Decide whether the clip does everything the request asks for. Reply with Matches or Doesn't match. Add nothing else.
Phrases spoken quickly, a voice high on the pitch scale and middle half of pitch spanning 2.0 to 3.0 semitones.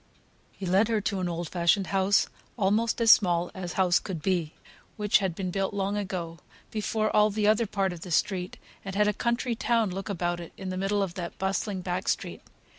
Matches